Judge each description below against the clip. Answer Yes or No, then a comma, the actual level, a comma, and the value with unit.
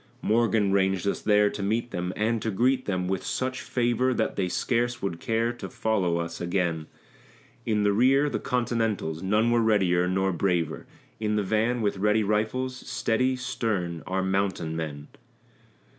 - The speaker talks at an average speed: Yes, average, 165 wpm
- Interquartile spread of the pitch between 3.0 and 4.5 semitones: Yes, average, 4.1 semitones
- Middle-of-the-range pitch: No, low, 105 Hz